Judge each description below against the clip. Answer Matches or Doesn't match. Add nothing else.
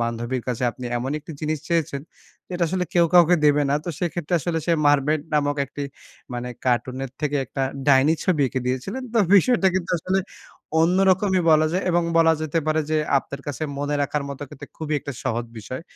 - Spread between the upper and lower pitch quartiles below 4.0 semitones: Doesn't match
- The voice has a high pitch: Doesn't match